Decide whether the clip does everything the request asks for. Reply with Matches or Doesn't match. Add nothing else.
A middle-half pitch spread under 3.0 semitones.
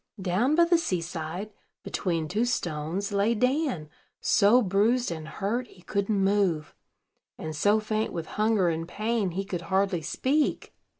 Doesn't match